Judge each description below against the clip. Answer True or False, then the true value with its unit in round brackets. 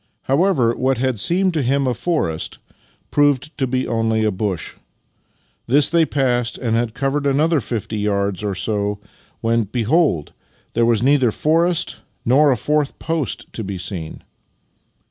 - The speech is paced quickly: False (155 wpm)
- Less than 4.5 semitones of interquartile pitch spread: False (5.0 semitones)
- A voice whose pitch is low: True (125 Hz)